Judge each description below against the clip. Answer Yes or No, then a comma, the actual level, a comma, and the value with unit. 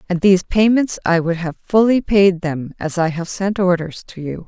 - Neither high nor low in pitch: Yes, medium, 180 Hz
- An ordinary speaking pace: No, fast, 215 wpm